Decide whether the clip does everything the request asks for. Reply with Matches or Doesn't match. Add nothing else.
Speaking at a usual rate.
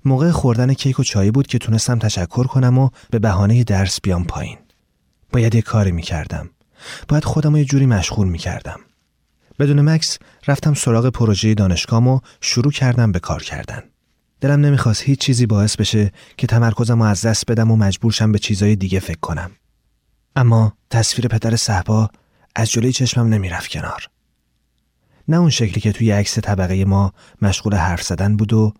Doesn't match